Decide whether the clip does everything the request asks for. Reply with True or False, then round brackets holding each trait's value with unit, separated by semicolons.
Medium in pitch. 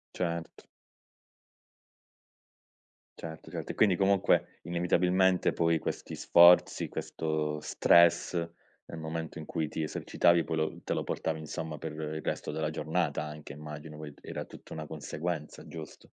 False (80 Hz)